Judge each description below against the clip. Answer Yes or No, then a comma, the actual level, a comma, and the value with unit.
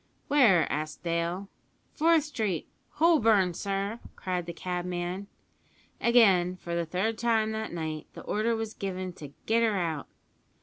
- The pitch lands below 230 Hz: Yes, high, 190 Hz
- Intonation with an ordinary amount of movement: Yes, average, 4.2 semitones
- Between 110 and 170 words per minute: Yes, average, 140 wpm